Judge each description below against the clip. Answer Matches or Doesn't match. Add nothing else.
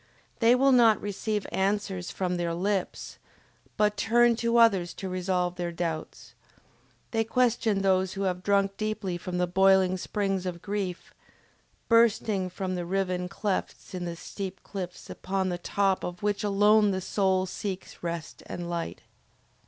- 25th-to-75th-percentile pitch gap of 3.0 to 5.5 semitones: Doesn't match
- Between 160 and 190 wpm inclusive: Doesn't match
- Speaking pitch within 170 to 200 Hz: Matches